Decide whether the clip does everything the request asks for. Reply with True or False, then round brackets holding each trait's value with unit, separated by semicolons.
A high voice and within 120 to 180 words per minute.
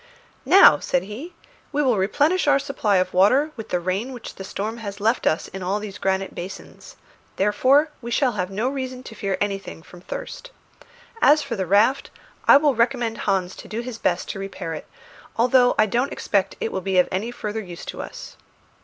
False (215 Hz; 200 wpm)